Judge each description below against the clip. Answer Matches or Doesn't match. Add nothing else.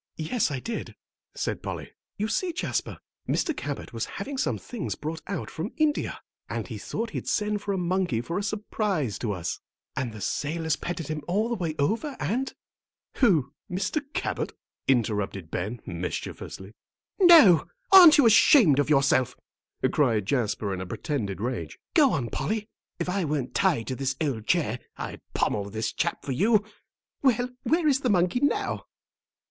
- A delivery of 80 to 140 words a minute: Doesn't match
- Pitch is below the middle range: Doesn't match